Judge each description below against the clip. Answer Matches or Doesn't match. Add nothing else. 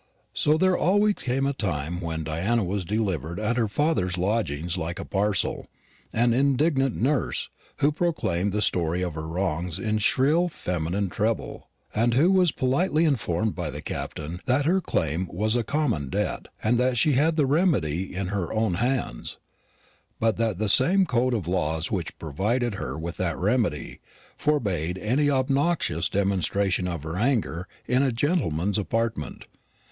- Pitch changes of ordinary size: Doesn't match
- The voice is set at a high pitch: Doesn't match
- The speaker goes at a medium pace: Matches